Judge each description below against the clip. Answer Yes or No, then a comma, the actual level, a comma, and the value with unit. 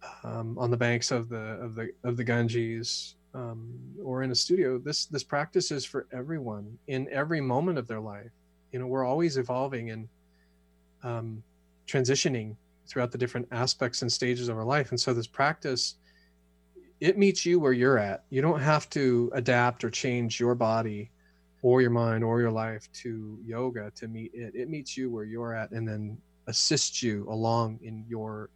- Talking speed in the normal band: Yes, average, 185 wpm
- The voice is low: Yes, low, 120 Hz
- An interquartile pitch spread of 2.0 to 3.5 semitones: Yes, average, 2.8 semitones